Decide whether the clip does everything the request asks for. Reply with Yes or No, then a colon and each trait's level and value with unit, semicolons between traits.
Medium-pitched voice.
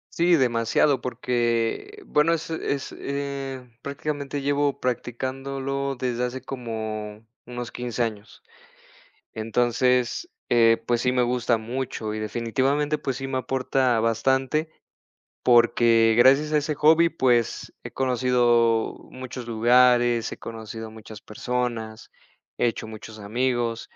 No: low, 125 Hz